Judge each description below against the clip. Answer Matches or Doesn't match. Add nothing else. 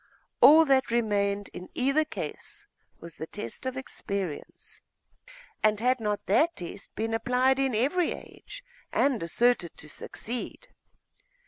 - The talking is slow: Matches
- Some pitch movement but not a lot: Matches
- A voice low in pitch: Doesn't match